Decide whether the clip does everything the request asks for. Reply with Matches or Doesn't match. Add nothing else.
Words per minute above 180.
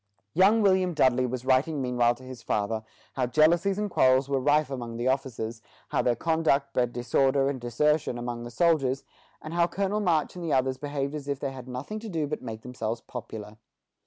Matches